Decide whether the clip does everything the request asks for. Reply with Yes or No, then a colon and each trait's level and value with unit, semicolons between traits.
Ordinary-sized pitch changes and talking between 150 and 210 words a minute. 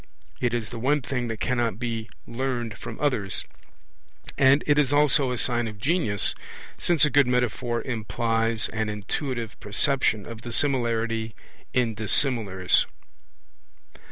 No: average, 3.0 semitones; slow, 135 wpm